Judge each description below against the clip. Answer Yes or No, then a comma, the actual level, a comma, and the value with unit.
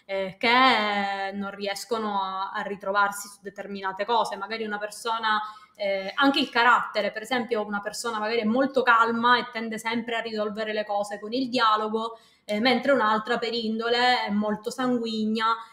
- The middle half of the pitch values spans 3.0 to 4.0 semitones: No, narrow, 2.4 semitones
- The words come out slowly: No, average, 165 wpm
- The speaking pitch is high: Yes, high, 220 Hz